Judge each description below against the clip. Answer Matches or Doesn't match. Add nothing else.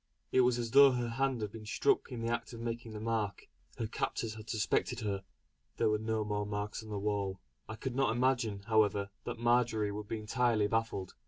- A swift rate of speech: Matches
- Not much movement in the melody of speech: Matches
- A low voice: Matches